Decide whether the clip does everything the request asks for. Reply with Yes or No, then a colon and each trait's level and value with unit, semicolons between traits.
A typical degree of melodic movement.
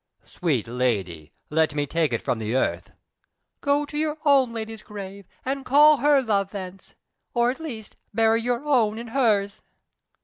No: wide, 8.2 semitones